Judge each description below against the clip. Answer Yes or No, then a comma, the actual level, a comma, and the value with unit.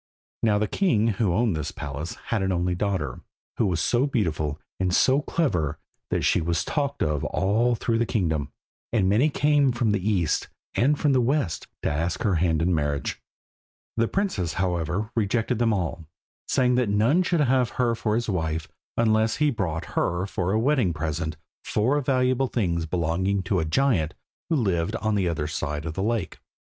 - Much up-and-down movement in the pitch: Yes, wide, 6.3 semitones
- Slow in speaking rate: No, average, 185 wpm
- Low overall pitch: Yes, low, 100 Hz